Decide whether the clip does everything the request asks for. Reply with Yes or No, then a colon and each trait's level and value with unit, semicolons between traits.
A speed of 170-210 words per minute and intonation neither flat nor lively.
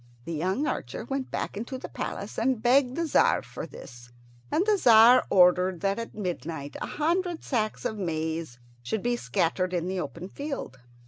No: average, 180 wpm; wide, 7.3 semitones